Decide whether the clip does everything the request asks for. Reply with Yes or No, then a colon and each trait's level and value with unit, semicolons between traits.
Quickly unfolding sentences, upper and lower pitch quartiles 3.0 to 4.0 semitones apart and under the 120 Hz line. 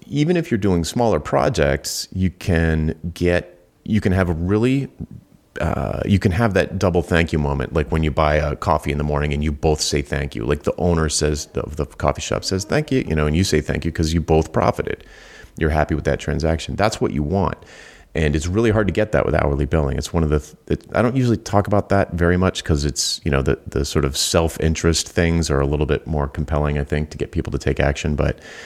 Yes: fast, 250 wpm; average, 3.6 semitones; very low, 80 Hz